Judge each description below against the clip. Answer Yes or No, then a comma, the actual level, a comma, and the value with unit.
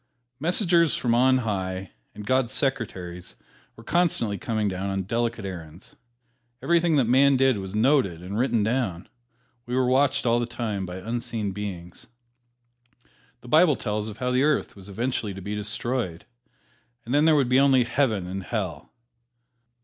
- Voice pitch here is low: Yes, low, 115 Hz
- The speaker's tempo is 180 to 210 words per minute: No, average, 160 wpm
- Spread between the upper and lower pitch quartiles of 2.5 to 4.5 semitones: No, average, 5.1 semitones